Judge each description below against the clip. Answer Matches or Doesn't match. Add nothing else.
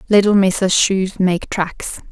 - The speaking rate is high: Doesn't match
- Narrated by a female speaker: Matches